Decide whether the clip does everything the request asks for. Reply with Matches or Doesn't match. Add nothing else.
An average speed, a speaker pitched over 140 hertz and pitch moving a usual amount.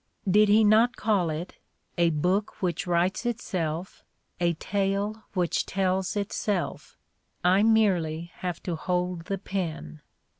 Doesn't match